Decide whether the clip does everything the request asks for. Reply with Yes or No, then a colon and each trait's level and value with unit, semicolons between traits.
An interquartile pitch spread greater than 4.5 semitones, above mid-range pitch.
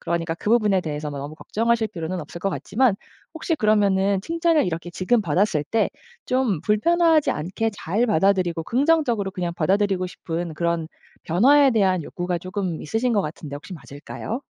Yes: average, 5.1 semitones; high, 195 Hz